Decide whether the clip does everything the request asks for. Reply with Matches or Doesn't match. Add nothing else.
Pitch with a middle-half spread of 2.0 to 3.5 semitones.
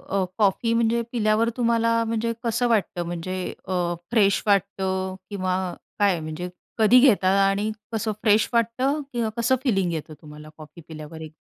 Doesn't match